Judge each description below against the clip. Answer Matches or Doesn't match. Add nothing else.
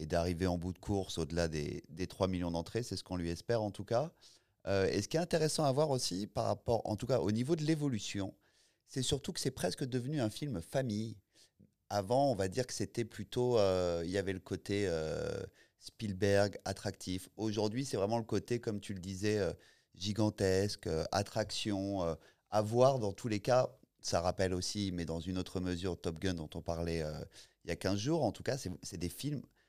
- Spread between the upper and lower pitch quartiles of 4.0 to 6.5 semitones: Matches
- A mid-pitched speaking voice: Doesn't match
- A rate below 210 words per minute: Doesn't match